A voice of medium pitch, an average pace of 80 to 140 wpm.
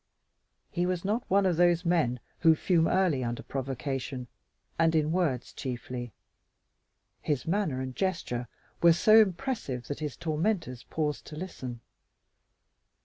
Yes: medium, 160 Hz; slow, 135 wpm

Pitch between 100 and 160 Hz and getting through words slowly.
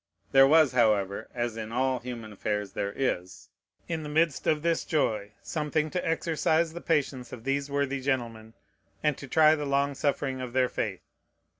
No: low, 135 Hz; average, 175 wpm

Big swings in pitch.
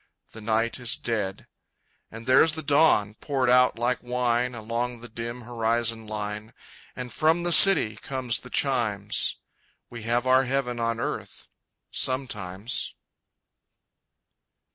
No: narrow, 2.4 semitones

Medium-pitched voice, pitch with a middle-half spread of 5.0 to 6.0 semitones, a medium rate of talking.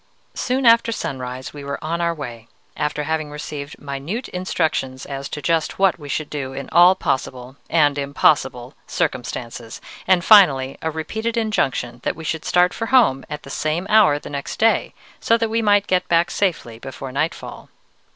Yes: medium, 150 Hz; average, 5.3 semitones; average, 175 wpm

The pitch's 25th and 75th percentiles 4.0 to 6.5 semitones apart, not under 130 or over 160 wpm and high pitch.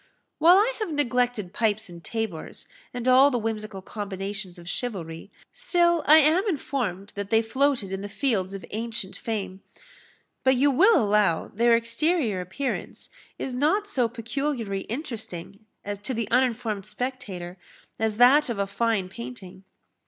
Yes: average, 5.1 semitones; average, 145 wpm; high, 225 Hz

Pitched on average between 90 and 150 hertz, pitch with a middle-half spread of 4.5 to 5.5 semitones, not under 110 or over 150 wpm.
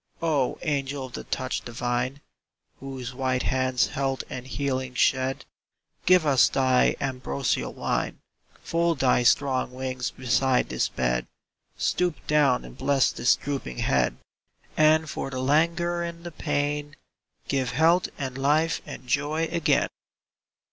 No: low, 135 Hz; average, 2.9 semitones; average, 140 wpm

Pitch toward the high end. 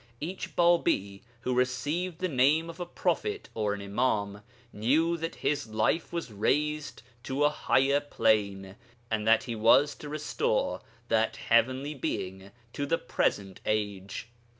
No: low, 130 Hz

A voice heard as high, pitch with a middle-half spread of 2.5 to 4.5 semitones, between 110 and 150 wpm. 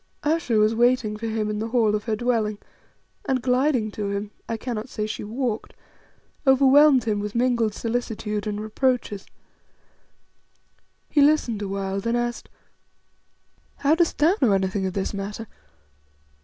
Yes: high, 225 Hz; average, 3.2 semitones; average, 145 wpm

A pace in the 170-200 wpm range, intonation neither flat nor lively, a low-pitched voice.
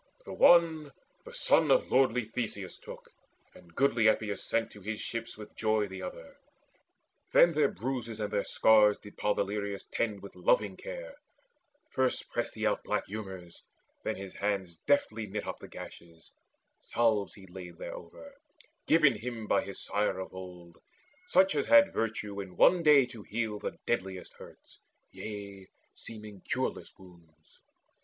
No: average, 155 wpm; average, 4.4 semitones; low, 105 Hz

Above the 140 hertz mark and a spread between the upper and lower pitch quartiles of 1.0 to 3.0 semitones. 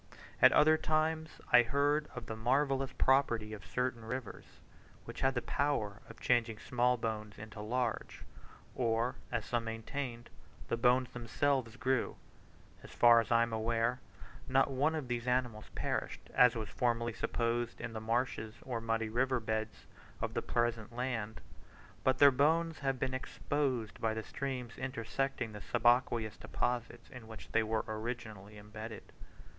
No: low, 120 Hz; average, 2.7 semitones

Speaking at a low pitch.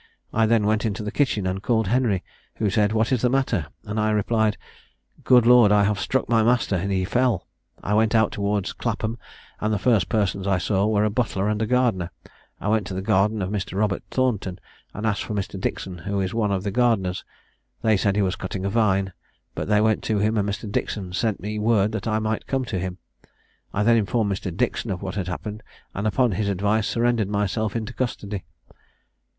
Yes: low, 105 Hz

